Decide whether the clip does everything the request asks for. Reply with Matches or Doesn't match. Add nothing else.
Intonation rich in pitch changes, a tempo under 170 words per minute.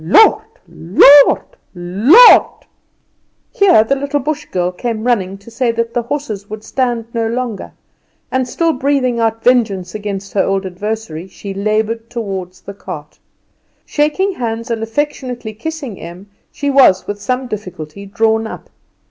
Doesn't match